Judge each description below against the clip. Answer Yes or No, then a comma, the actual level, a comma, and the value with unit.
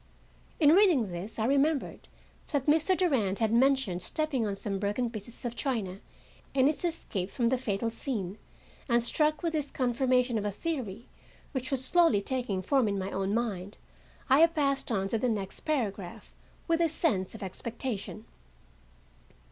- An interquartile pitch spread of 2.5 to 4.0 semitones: No, wide, 5.6 semitones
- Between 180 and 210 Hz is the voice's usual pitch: No, high, 240 Hz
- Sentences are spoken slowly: No, average, 165 wpm